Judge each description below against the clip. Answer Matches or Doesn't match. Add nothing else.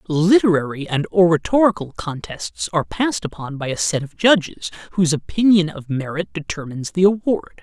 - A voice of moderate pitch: Matches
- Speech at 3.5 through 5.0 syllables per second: Doesn't match